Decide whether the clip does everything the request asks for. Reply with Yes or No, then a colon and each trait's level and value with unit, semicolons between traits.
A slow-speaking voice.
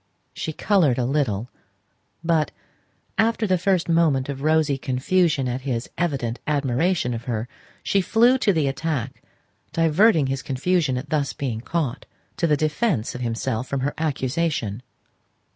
No: average, 145 wpm